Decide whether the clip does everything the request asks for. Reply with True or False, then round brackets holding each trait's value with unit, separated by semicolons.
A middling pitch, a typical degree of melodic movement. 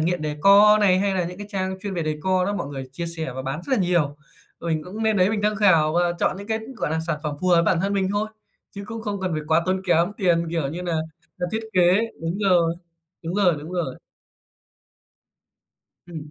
True (180 Hz; 3.4 semitones)